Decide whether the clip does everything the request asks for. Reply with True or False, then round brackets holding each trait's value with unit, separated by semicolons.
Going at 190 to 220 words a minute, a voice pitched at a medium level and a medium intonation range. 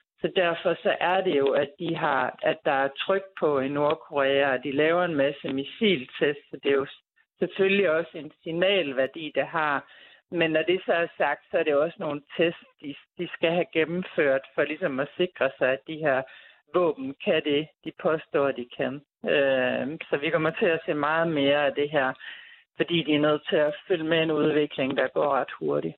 True (210 wpm; 155 Hz; 3.4 semitones)